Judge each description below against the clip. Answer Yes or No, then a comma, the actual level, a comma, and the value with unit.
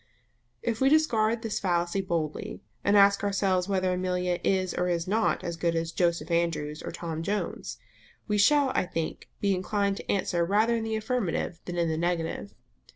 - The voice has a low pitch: No, medium, 185 Hz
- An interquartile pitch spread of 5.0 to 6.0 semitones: No, average, 3.4 semitones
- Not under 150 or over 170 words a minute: No, average, 180 wpm